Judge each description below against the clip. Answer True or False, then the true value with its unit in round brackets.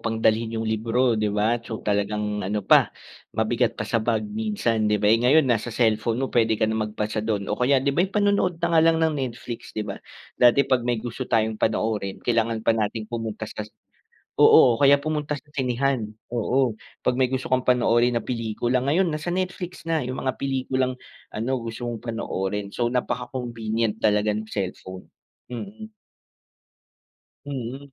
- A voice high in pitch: False (120 Hz)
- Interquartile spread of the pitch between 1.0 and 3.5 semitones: True (3.2 semitones)